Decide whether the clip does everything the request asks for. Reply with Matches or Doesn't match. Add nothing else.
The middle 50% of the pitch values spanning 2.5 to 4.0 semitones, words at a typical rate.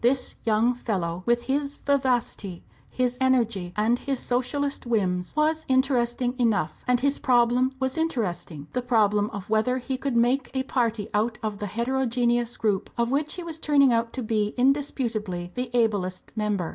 Matches